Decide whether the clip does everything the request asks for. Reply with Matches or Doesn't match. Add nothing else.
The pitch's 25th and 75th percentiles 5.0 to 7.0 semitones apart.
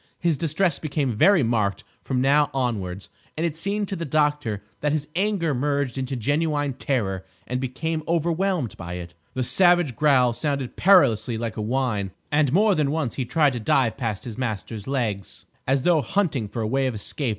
Matches